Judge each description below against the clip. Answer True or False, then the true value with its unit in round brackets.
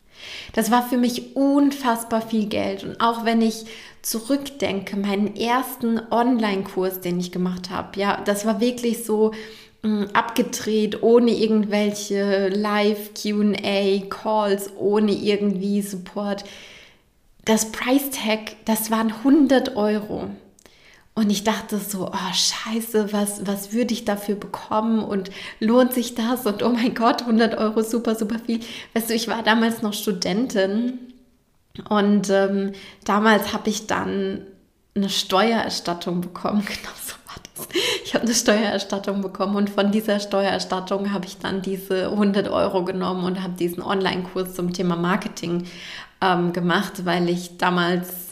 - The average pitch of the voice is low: False (210 Hz)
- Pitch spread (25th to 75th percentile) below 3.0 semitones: True (2.5 semitones)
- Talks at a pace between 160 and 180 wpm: False (140 wpm)